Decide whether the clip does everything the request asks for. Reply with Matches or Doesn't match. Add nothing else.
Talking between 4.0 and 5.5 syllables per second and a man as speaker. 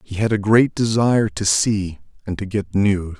Matches